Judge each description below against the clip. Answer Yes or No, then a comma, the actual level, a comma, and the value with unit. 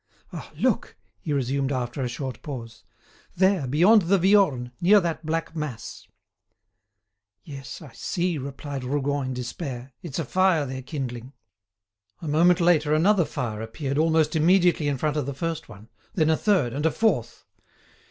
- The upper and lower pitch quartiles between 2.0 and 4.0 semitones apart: No, average, 4.4 semitones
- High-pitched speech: No, medium, 150 Hz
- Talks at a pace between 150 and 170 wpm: Yes, average, 160 wpm